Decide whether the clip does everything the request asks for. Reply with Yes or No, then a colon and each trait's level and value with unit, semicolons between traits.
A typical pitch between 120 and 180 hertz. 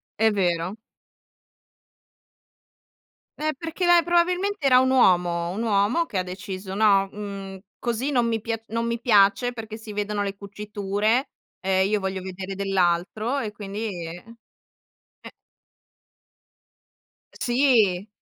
No: high, 210 Hz